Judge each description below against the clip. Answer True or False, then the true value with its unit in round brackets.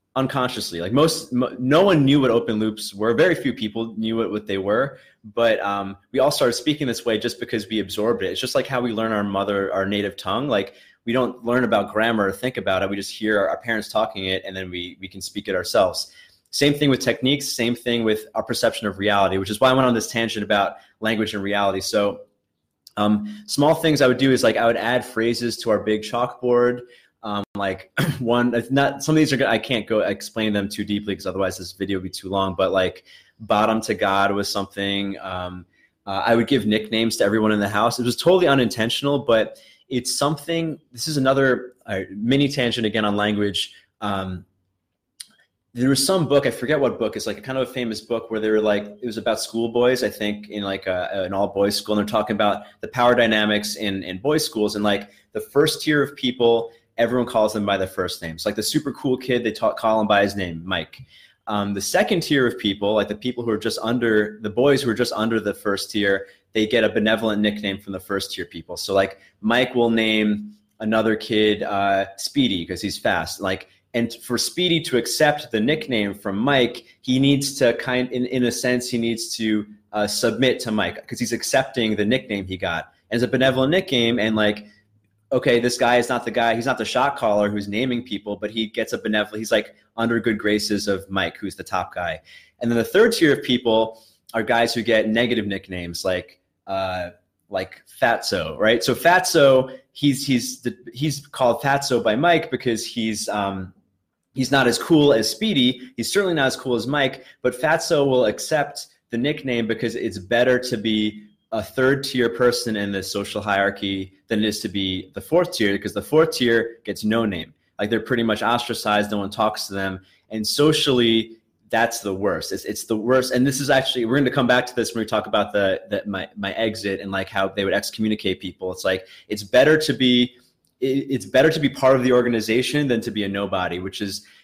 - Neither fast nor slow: False (225 wpm)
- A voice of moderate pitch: False (110 Hz)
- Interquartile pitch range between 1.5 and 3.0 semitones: False (3.5 semitones)